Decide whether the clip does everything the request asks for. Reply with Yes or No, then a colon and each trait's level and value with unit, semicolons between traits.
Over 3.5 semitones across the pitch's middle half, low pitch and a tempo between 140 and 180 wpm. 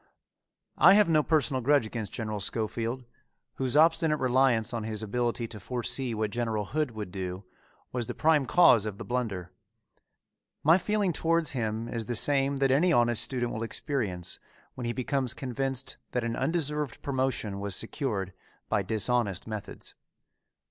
Yes: average, 4.2 semitones; low, 120 Hz; average, 155 wpm